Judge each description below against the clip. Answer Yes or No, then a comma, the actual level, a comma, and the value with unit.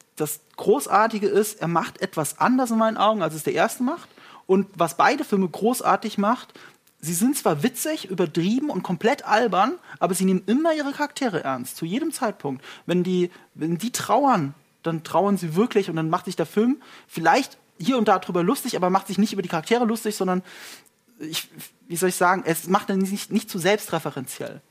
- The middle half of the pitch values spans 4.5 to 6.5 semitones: Yes, average, 5.0 semitones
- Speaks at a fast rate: Yes, fast, 195 wpm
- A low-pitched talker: No, high, 200 Hz